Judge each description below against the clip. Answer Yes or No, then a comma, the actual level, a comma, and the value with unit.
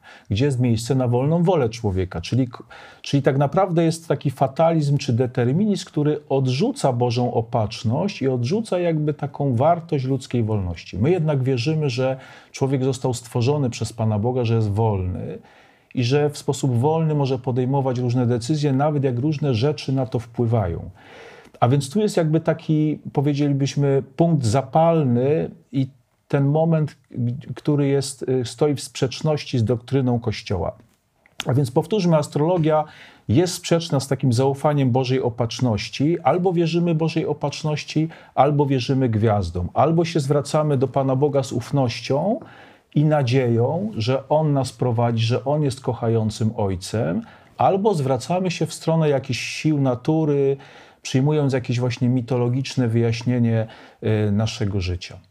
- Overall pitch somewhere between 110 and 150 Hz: Yes, low, 135 Hz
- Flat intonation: No, average, 3.7 semitones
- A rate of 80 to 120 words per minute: No, average, 140 wpm